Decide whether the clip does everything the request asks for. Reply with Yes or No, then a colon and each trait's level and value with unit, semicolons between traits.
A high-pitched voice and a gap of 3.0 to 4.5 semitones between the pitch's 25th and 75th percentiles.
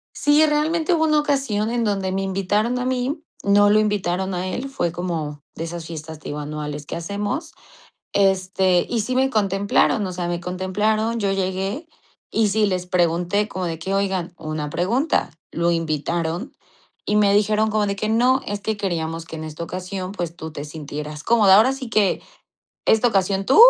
Yes: high, 195 Hz; average, 4.2 semitones